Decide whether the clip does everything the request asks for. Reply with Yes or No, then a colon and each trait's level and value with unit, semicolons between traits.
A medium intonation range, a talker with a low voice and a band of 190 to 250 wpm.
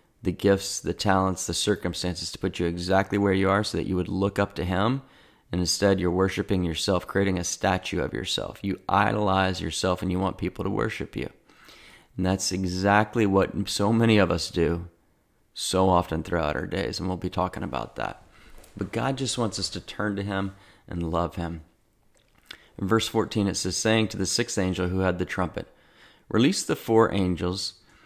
No: narrow, 2.3 semitones; very low, 95 Hz; average, 195 wpm